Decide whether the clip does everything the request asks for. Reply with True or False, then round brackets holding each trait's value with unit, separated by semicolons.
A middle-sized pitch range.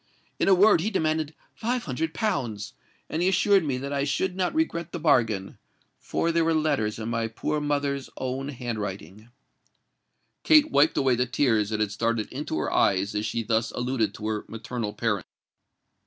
False (6.3 semitones)